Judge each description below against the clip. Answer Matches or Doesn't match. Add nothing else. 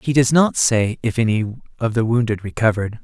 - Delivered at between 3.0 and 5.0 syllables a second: Doesn't match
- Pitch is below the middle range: Matches